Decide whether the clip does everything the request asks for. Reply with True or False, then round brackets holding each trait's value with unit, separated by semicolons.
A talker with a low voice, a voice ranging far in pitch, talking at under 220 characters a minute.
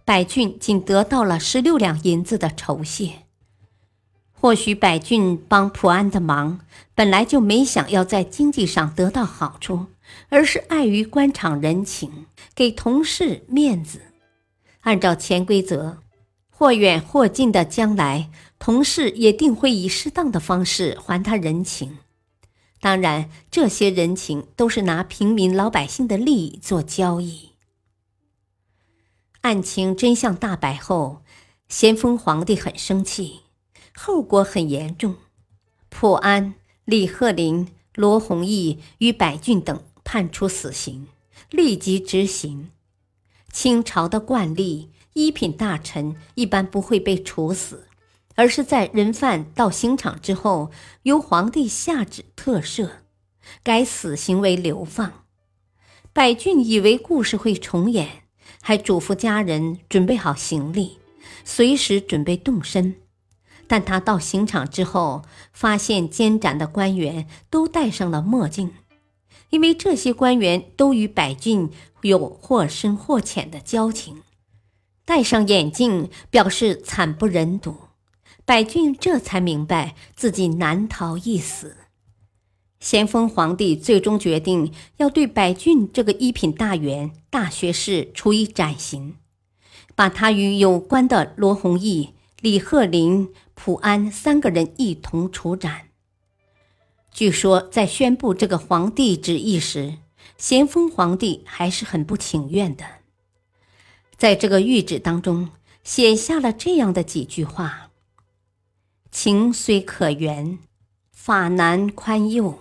False (185 Hz; 6.3 semitones; 190 characters per minute)